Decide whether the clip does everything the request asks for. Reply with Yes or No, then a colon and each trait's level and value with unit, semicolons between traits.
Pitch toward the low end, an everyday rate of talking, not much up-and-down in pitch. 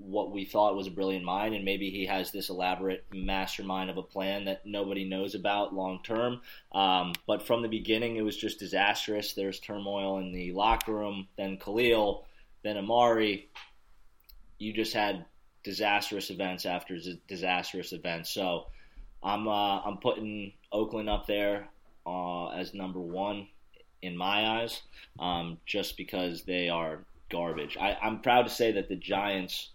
Yes: low, 100 Hz; average, 160 wpm; narrow, 2.1 semitones